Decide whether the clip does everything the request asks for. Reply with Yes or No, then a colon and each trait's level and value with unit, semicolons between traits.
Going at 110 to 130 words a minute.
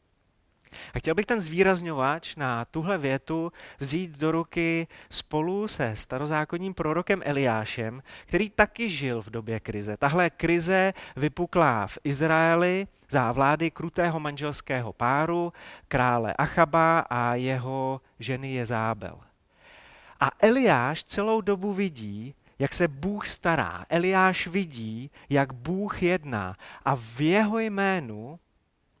Yes: slow, 115 wpm